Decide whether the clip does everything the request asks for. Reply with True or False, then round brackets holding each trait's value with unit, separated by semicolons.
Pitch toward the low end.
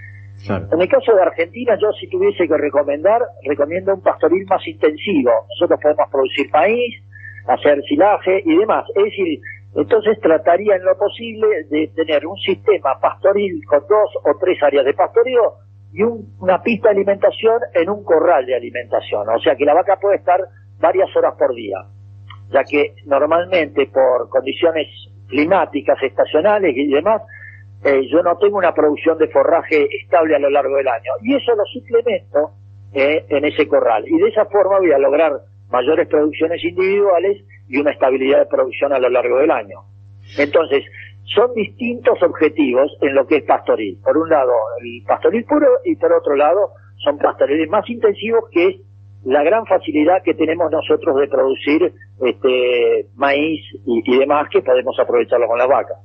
False (170 Hz)